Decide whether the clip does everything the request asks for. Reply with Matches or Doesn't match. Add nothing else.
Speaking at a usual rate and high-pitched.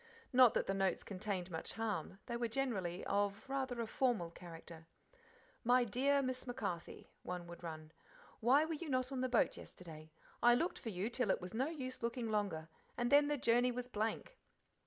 Matches